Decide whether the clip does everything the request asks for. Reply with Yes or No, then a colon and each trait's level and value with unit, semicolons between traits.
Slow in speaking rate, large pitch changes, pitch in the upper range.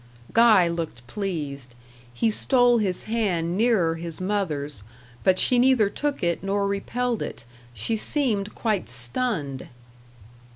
Yes: slow, 125 wpm; wide, 5.8 semitones; high, 195 Hz